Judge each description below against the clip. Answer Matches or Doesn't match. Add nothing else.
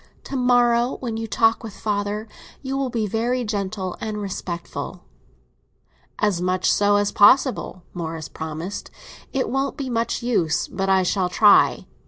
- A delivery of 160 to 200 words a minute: Doesn't match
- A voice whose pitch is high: Matches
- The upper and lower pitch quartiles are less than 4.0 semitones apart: Doesn't match